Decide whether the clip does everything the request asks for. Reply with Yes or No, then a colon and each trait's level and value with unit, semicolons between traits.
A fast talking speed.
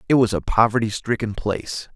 No: average, 185 wpm